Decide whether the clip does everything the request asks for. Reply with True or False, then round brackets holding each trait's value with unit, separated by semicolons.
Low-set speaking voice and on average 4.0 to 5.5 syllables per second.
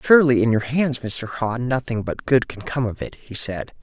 True (120 Hz; 4.9 syllables/s)